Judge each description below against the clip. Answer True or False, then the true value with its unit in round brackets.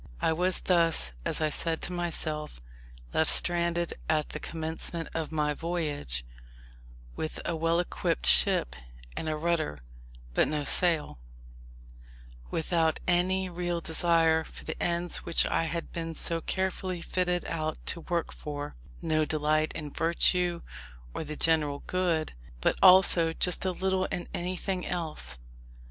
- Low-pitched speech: False (165 Hz)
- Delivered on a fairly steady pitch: True (2.1 semitones)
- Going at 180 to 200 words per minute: False (140 wpm)